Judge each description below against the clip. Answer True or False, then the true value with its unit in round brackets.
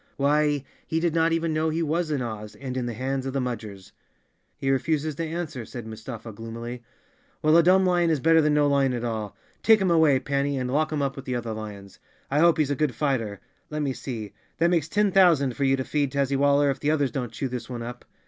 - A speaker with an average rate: False (240 wpm)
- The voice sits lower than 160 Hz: True (140 Hz)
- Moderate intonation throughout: True (4.3 semitones)